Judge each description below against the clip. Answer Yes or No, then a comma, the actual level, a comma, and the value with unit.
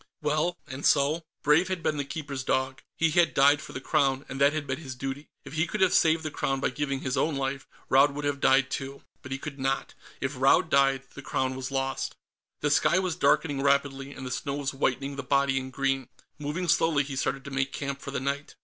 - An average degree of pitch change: No, narrow, 1.7 semitones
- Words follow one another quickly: Yes, fast, 235 wpm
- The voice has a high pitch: No, medium, 140 Hz